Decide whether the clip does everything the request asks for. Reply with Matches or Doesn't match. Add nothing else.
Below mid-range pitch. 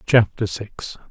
Matches